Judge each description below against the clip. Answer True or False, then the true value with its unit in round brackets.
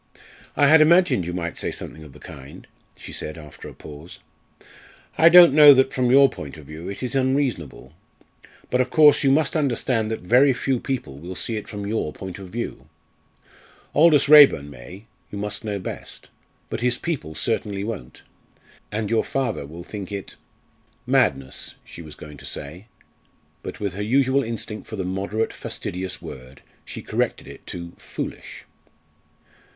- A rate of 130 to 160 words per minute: False (170 wpm)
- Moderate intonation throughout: False (7.6 semitones)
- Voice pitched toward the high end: False (105 Hz)